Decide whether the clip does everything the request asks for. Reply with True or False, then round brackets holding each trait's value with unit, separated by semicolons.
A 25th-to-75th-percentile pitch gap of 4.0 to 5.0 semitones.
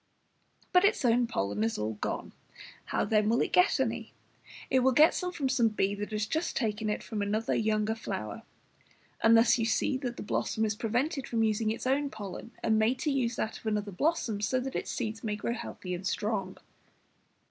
False (3.4 semitones)